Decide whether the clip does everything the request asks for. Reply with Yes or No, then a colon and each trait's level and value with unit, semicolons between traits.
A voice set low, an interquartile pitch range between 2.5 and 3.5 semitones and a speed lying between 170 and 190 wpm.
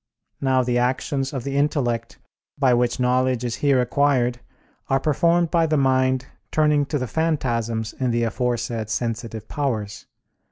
No: low, 130 Hz; average, 3.1 semitones; average, 150 wpm